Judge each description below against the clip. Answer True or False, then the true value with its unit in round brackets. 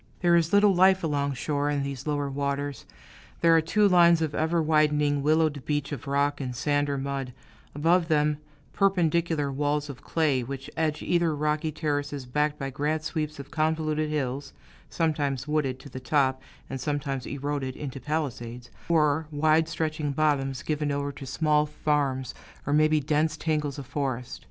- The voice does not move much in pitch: True (2.0 semitones)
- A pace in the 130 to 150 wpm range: False (165 wpm)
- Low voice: False (150 Hz)